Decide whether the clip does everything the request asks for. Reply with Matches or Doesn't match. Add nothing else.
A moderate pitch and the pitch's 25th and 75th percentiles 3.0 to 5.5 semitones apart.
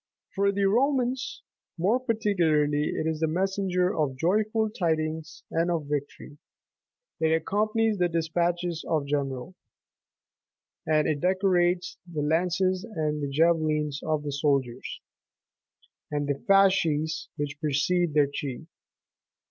Matches